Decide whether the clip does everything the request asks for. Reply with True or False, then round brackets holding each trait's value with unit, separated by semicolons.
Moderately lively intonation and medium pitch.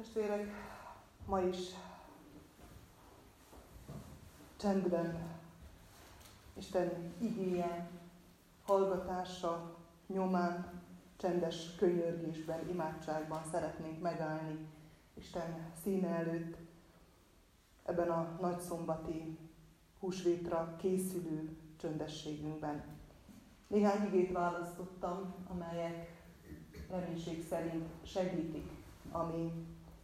False (2.2 semitones; 170 Hz)